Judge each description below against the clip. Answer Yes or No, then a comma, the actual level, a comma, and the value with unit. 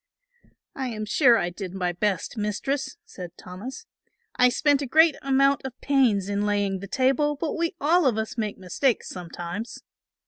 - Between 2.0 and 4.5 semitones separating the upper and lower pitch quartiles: No, wide, 5.6 semitones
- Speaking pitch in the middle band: No, high, 230 Hz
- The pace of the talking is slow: No, average, 170 wpm